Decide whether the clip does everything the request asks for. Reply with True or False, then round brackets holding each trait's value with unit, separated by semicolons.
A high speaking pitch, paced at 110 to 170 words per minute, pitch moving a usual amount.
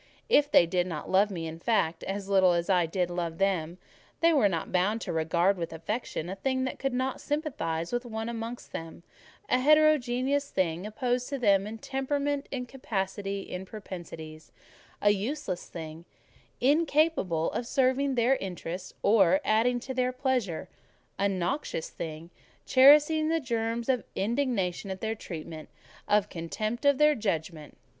False (210 Hz; 155 wpm; 6.7 semitones)